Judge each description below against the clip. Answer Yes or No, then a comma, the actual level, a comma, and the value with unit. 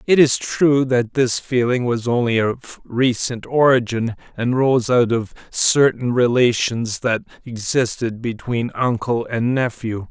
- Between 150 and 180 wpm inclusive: No, slow, 135 wpm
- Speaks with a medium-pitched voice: No, low, 120 Hz